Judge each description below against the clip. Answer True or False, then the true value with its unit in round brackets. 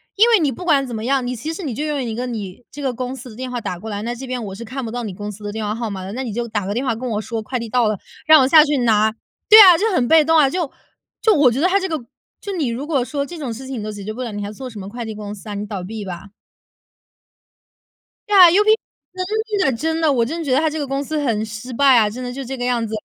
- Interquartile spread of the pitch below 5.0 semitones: False (5.3 semitones)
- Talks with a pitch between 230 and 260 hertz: True (250 Hz)